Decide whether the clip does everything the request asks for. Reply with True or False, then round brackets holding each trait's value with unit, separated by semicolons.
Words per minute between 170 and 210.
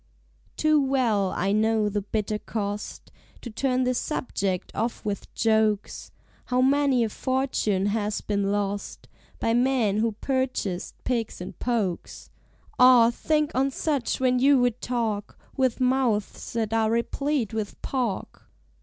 False (135 wpm)